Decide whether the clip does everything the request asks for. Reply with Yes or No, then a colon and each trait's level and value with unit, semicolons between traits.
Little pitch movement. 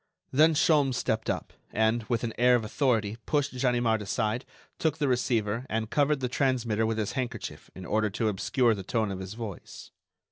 No: average, 3.1 semitones